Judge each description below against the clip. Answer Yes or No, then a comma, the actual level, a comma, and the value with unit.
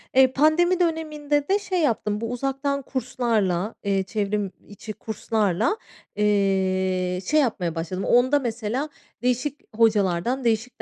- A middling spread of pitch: No, wide, 5.8 semitones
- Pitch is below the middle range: No, high, 230 Hz